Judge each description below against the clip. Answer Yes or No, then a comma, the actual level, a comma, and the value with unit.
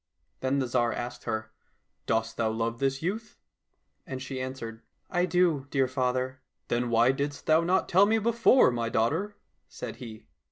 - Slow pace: No, average, 200 wpm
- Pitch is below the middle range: Yes, low, 130 Hz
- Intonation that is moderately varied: No, wide, 6.1 semitones